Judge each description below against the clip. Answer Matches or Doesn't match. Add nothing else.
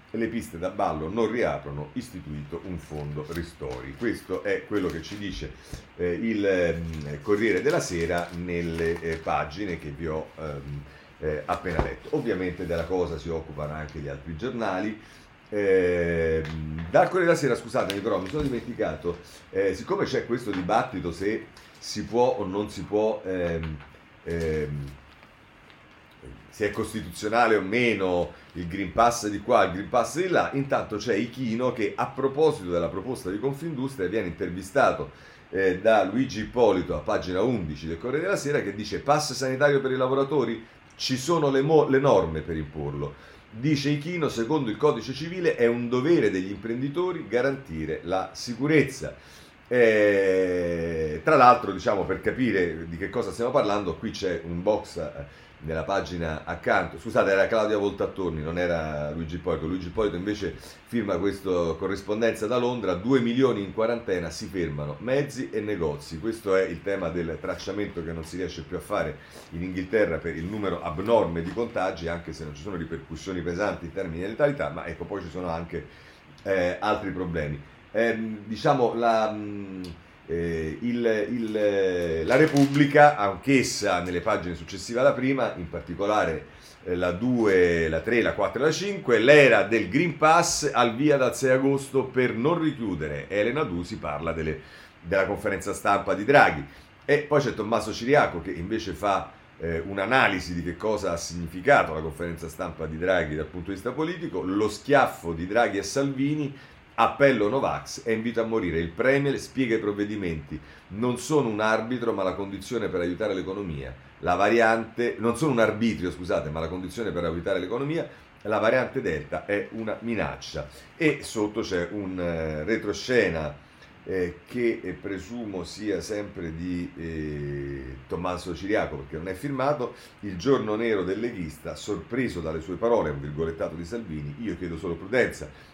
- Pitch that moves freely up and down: Matches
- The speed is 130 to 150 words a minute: Doesn't match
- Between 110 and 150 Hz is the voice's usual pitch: Doesn't match